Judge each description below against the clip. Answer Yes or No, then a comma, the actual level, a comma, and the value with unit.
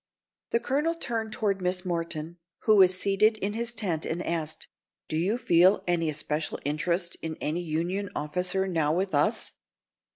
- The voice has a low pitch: No, medium, 180 Hz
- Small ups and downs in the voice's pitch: No, average, 3.8 semitones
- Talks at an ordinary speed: Yes, average, 160 wpm